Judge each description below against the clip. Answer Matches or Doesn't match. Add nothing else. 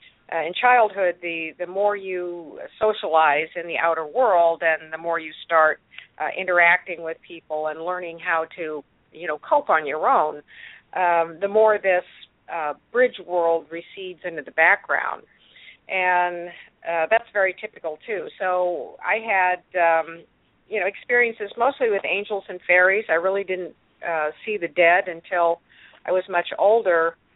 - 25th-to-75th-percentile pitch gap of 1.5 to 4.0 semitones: Matches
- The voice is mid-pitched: Matches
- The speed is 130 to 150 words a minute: Doesn't match